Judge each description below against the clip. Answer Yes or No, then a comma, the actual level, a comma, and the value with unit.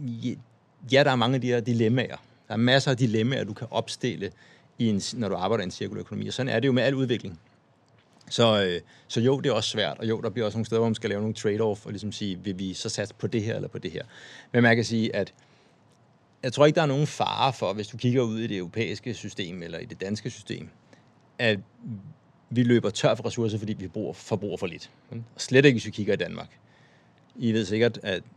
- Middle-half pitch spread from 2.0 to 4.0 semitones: Yes, average, 3.0 semitones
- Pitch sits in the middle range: No, low, 115 Hz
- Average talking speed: No, fast, 245 wpm